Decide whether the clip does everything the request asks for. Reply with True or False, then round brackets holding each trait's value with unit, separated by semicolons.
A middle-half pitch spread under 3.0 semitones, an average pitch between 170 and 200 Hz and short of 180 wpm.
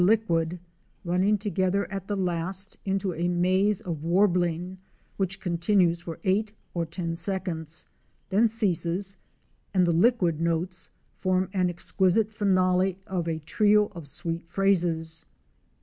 True (2.6 semitones; 185 Hz; 135 wpm)